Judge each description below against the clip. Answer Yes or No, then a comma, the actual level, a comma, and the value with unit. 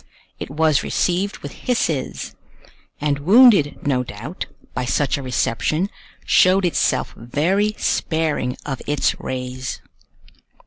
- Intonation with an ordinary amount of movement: No, wide, 6.0 semitones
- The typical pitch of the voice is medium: Yes, medium, 150 Hz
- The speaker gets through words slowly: Yes, slow, 115 wpm